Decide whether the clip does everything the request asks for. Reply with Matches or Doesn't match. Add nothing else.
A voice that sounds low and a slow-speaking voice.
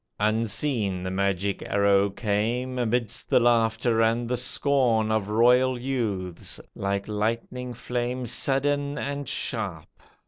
Matches